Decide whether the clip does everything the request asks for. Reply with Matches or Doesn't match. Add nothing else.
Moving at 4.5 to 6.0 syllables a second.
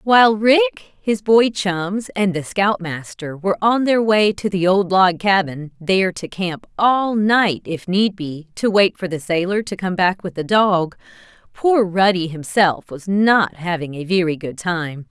Doesn't match